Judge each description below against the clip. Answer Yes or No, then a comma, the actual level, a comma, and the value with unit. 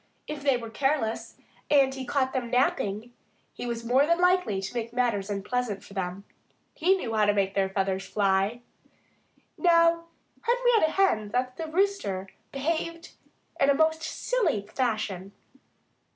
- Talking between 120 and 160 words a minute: Yes, average, 150 wpm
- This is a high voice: Yes, very high, 250 Hz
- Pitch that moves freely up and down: Yes, wide, 7.5 semitones